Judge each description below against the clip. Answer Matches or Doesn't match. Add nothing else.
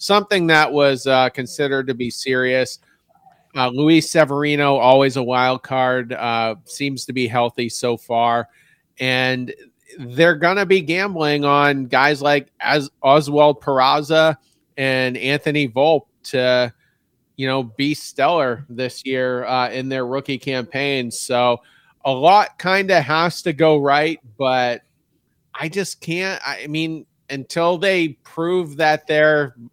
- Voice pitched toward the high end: Doesn't match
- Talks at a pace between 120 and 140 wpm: Matches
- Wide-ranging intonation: Doesn't match